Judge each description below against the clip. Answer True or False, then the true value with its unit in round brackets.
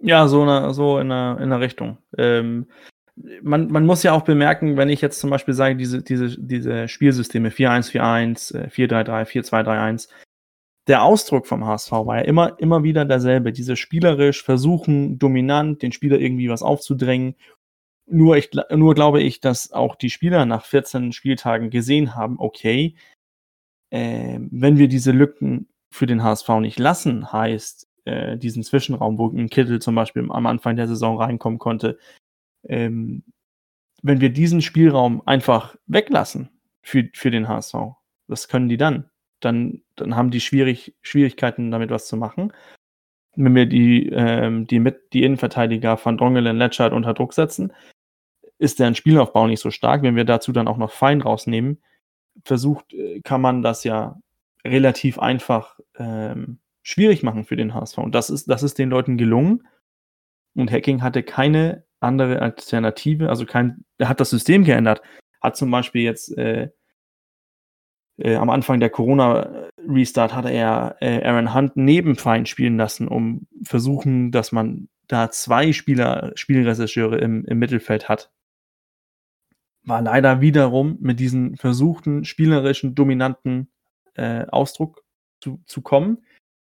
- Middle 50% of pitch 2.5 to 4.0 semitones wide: True (3.4 semitones)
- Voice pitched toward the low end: True (125 Hz)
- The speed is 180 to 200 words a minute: False (150 wpm)